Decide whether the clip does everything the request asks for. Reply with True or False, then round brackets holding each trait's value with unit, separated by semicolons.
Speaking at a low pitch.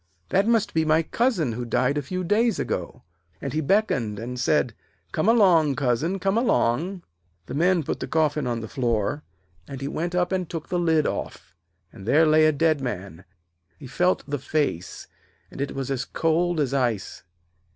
False (155 Hz)